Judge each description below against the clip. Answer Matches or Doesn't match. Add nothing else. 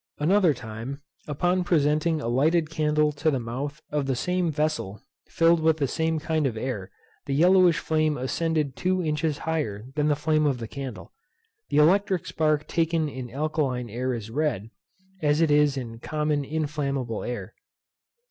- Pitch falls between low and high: Matches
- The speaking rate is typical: Matches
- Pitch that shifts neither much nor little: Matches